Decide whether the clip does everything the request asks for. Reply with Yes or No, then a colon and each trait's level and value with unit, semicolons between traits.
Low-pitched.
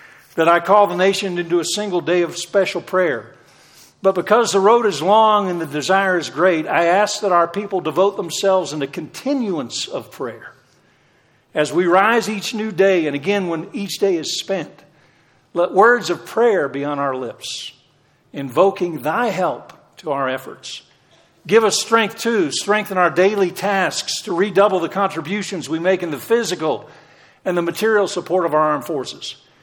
No: medium, 185 Hz